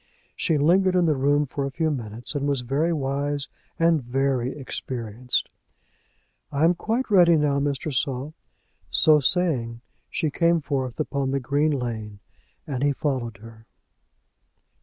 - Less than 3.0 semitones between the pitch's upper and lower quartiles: No, average, 3.4 semitones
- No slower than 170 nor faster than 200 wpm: No, average, 145 wpm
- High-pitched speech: No, medium, 140 Hz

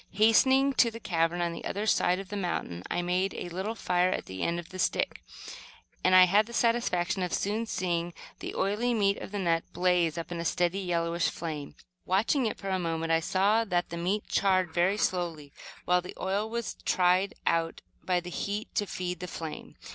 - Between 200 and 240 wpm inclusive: Yes, fast, 205 wpm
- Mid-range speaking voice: Yes, medium, 180 Hz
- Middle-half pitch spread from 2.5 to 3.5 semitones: Yes, average, 2.9 semitones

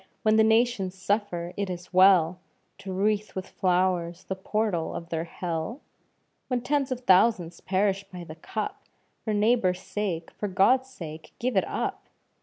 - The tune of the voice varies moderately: Yes, average, 3.5 semitones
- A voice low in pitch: No, high, 190 Hz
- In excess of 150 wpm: Yes, average, 160 wpm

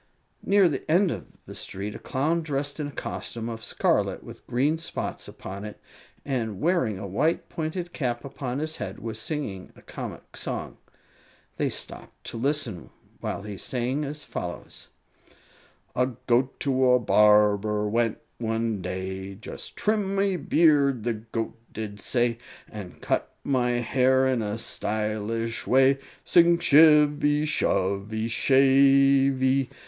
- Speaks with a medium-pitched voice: No, low, 125 Hz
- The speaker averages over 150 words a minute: No, average, 140 wpm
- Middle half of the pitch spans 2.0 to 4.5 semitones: No, average, 5.3 semitones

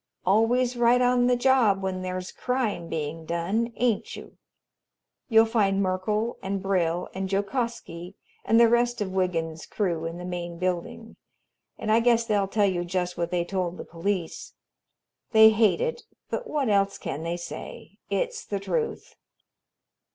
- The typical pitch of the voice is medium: No, high, 195 Hz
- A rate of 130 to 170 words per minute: Yes, average, 160 wpm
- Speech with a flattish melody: No, average, 4.7 semitones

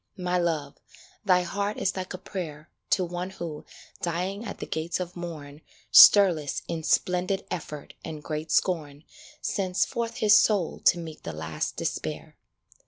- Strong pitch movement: No, average, 3.3 semitones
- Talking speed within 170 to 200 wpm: No, average, 155 wpm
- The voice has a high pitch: No, medium, 175 Hz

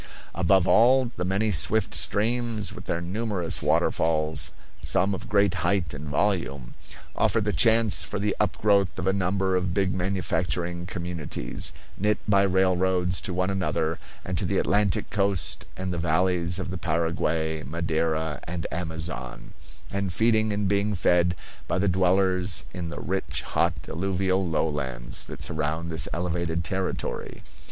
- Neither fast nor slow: Yes, average, 150 wpm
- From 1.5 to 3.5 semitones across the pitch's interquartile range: Yes, average, 2.9 semitones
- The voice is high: No, very low, 90 Hz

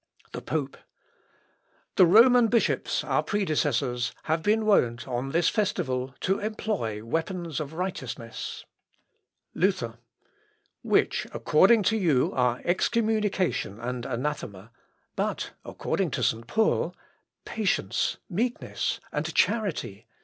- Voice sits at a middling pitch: Yes, medium, 165 Hz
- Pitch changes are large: Yes, wide, 8.8 semitones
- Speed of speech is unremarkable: No, slow, 110 wpm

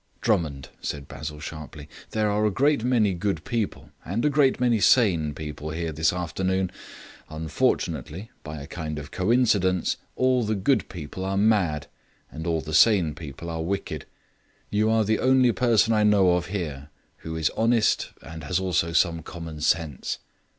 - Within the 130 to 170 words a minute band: Yes, average, 165 wpm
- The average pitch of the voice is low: Yes, very low, 90 Hz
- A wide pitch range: Yes, wide, 5.7 semitones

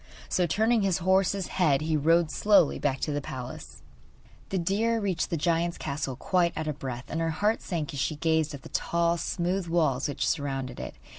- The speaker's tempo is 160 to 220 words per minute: Yes, average, 200 wpm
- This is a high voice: No, medium, 165 Hz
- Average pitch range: Yes, average, 4.1 semitones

